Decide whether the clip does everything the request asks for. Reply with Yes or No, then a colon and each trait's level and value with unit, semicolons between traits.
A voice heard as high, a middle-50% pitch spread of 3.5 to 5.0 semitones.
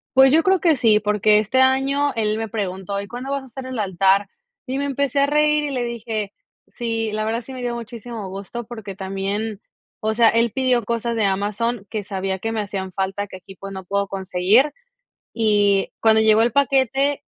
Yes: high, 220 Hz; average, 4.3 semitones